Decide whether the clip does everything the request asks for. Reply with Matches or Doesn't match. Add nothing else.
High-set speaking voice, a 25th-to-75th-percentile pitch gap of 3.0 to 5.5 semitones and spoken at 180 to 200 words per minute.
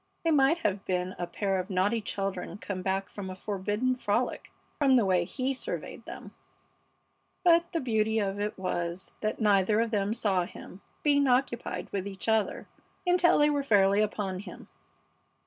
Doesn't match